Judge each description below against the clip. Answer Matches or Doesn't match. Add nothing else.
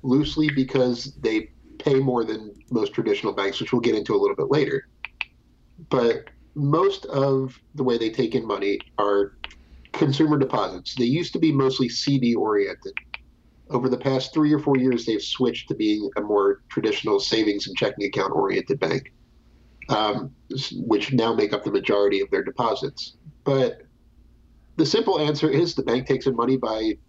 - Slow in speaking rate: Doesn't match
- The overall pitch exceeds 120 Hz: Matches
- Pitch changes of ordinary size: Doesn't match